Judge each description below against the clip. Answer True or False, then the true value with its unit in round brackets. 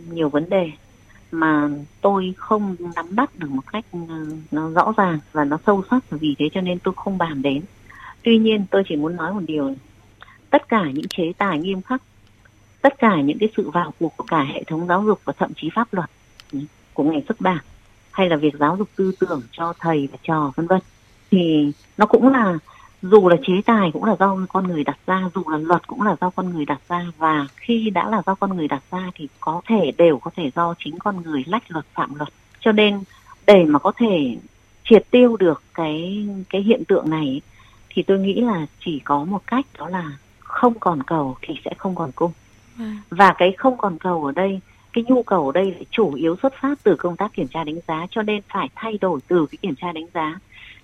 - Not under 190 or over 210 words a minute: False (225 wpm)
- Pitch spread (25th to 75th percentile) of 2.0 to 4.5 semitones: False (5.1 semitones)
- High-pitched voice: False (175 Hz)